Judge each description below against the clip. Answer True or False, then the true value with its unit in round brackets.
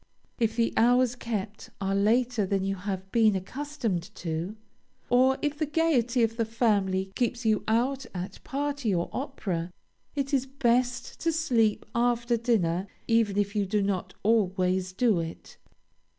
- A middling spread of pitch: True (4.3 semitones)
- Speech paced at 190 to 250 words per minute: False (150 wpm)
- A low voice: False (225 Hz)